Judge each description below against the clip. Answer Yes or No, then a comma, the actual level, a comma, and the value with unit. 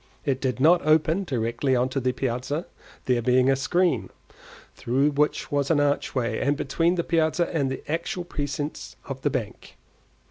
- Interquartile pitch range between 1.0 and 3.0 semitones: No, average, 3.4 semitones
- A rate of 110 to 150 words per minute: No, average, 165 wpm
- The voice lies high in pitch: No, medium, 140 Hz